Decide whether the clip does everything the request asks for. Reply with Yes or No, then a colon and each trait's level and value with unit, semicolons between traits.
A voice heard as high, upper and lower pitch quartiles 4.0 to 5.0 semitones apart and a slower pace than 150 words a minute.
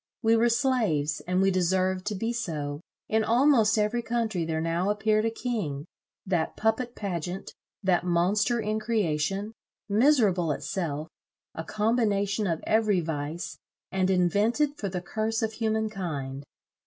Yes: high, 200 Hz; average, 4.4 semitones; average, 140 wpm